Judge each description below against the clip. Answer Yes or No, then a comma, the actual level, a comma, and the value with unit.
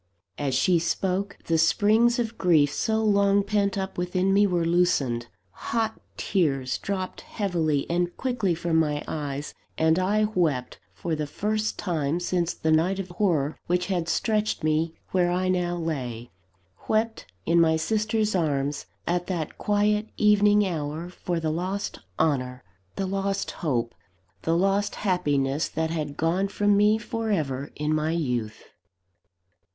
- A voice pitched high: No, medium, 175 Hz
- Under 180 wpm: Yes, average, 150 wpm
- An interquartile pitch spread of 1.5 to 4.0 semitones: No, average, 4.5 semitones